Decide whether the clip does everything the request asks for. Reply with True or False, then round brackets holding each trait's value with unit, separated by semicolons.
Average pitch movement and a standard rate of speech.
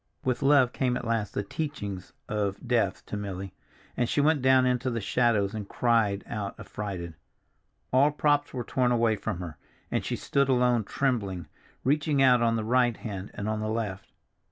True (4.0 semitones; 180 wpm)